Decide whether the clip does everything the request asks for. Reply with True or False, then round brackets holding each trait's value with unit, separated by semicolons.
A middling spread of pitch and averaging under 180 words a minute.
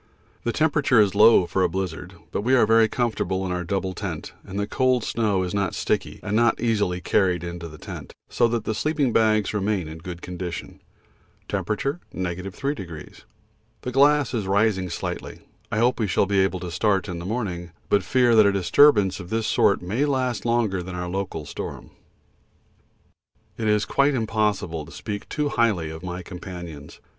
False (4.3 semitones; 185 wpm)